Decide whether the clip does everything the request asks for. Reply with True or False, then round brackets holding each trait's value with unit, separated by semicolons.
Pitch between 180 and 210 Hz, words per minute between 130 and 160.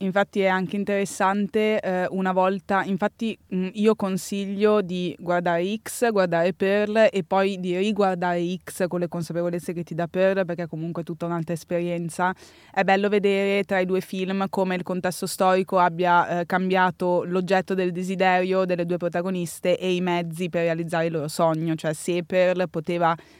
False (185 Hz; 170 wpm)